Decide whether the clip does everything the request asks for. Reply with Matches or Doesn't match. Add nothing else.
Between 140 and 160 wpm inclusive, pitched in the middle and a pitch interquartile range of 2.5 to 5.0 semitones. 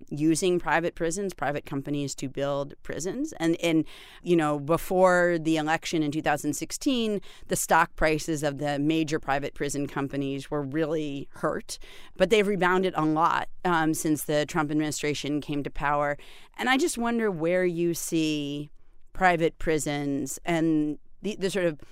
Matches